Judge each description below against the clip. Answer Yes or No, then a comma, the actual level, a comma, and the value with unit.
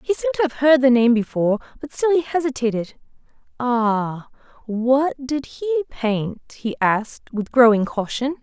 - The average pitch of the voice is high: Yes, very high, 255 Hz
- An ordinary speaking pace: Yes, average, 150 wpm